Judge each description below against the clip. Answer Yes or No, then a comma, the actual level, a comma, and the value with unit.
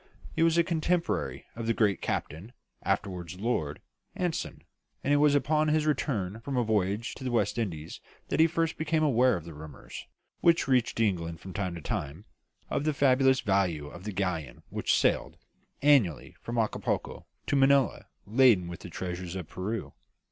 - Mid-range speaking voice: No, low, 115 Hz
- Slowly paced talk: No, average, 175 wpm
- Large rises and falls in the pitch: Yes, wide, 7.6 semitones